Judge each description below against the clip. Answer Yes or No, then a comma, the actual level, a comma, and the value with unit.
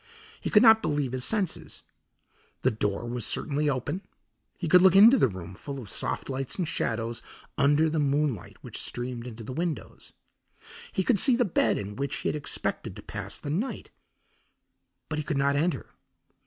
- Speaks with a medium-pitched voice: Yes, medium, 145 Hz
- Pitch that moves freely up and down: Yes, wide, 6.1 semitones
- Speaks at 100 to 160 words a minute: No, average, 180 wpm